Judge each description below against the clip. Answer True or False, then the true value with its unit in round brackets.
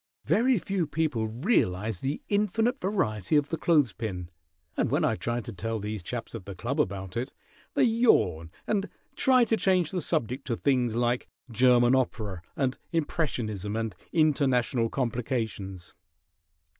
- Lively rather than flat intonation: True (7.0 semitones)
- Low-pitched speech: True (125 Hz)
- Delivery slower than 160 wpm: True (150 wpm)